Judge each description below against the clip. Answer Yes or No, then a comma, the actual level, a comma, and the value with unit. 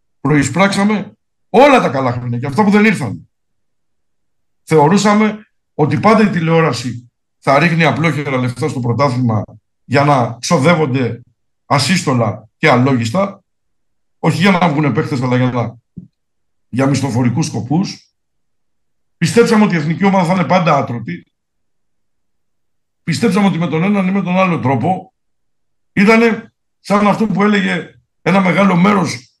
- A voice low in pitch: No, medium, 160 Hz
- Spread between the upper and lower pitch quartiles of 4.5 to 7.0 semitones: No, wide, 7.6 semitones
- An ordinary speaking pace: Yes, average, 135 wpm